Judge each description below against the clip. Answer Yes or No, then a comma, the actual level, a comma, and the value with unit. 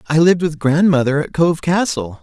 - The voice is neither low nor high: Yes, medium, 160 Hz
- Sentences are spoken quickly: No, average, 190 wpm